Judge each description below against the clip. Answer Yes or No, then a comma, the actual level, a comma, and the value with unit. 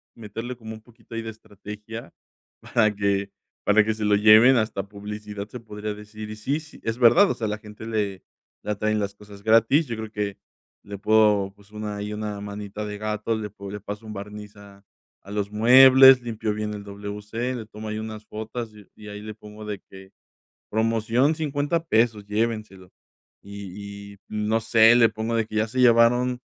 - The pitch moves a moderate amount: No, narrow, 1.6 semitones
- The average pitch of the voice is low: Yes, low, 105 Hz